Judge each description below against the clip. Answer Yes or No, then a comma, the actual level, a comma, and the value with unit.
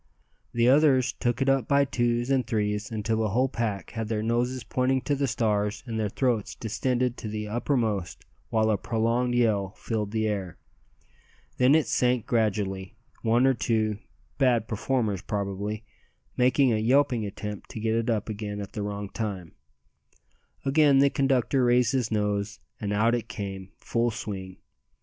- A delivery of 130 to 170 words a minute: Yes, average, 165 wpm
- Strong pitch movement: No, average, 3.2 semitones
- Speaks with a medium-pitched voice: No, low, 115 Hz